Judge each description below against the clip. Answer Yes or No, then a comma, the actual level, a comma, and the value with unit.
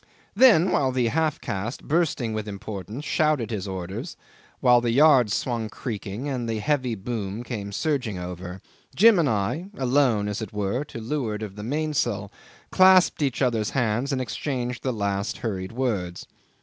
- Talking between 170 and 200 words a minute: No, average, 160 wpm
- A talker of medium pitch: No, low, 120 Hz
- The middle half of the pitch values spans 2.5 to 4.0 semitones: No, average, 5.1 semitones